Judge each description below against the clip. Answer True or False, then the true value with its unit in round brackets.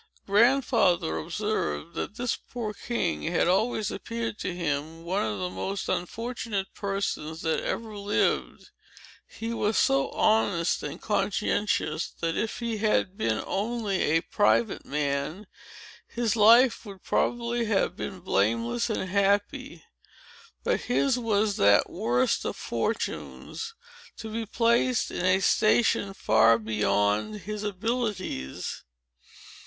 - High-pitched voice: True (200 Hz)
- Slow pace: True (125 wpm)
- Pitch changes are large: True (5.8 semitones)